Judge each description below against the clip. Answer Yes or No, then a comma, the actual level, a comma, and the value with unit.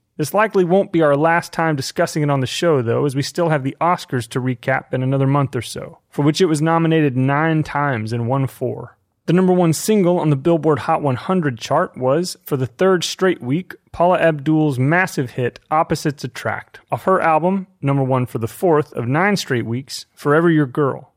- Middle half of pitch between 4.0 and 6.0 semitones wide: Yes, average, 4.3 semitones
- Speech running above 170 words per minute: Yes, fast, 205 wpm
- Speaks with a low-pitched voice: No, medium, 150 Hz